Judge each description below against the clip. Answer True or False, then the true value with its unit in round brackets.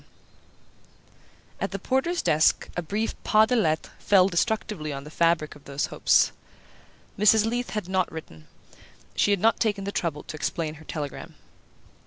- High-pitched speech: False (180 Hz)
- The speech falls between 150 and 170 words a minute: True (165 wpm)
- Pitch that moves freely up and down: True (5.7 semitones)